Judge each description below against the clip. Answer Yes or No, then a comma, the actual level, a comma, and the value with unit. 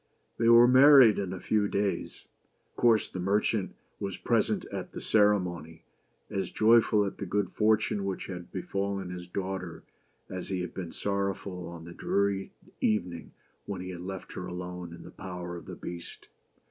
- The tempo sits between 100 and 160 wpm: No, average, 170 wpm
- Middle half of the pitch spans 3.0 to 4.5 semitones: No, narrow, 2.4 semitones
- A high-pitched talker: No, very low, 95 Hz